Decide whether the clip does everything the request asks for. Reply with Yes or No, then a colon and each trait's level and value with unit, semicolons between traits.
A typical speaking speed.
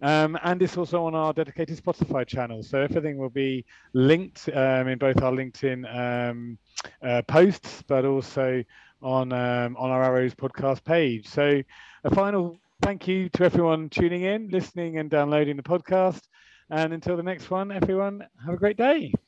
Yes: average, 170 wpm